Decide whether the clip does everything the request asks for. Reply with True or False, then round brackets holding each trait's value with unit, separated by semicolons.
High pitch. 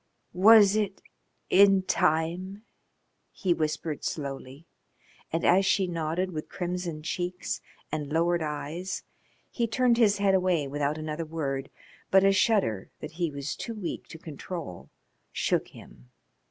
False (170 Hz)